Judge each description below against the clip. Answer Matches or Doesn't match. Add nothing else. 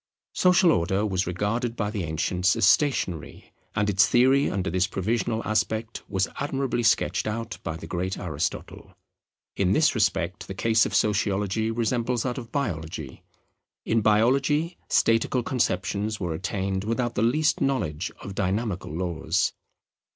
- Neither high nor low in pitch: Doesn't match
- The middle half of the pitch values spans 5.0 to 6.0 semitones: Doesn't match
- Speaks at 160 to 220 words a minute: Doesn't match